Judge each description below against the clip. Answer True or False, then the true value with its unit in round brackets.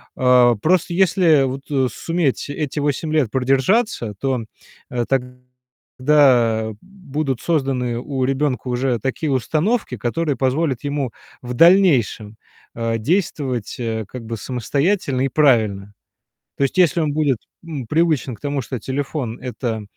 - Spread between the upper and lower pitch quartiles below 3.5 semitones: False (3.8 semitones)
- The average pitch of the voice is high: False (135 Hz)